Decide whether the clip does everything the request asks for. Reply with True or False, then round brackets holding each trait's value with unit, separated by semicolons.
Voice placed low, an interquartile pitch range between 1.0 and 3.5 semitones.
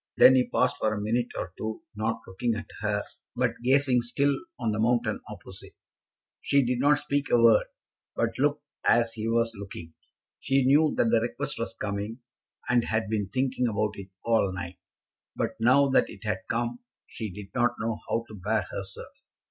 True (115 Hz; 2.7 semitones)